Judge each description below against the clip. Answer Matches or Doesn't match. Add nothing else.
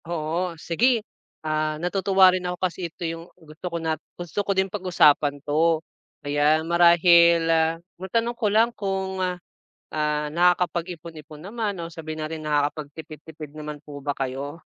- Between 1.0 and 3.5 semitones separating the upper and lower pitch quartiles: Matches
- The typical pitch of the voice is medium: Matches